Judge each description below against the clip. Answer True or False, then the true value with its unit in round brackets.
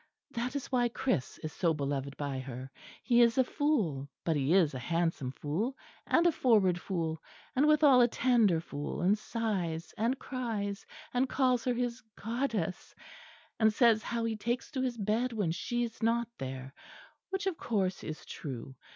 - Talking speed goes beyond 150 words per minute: True (175 wpm)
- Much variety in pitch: True (7.3 semitones)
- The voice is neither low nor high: False (220 Hz)